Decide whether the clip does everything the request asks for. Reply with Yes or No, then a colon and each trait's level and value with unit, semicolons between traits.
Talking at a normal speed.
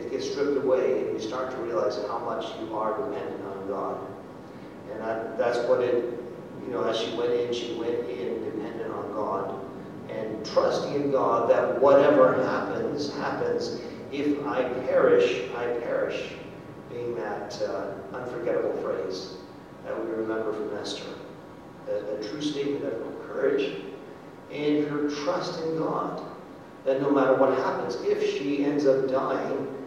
Yes: average, 150 wpm